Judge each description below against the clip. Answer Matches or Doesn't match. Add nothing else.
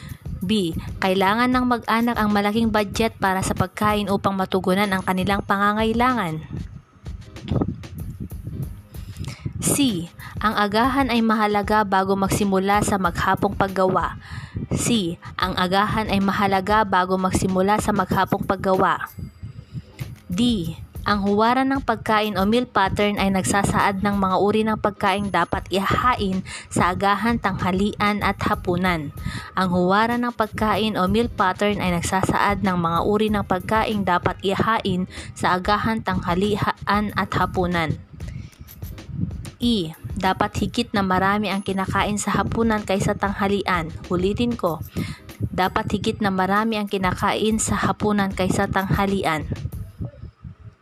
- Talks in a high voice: Matches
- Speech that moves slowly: Matches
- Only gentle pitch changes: Matches